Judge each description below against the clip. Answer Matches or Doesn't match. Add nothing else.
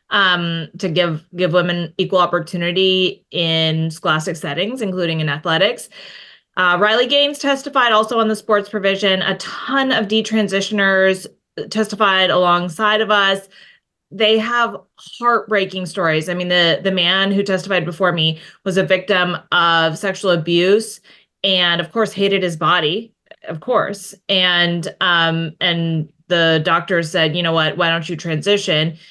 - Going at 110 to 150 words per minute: Matches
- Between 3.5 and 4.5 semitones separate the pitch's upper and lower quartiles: Doesn't match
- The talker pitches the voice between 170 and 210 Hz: Matches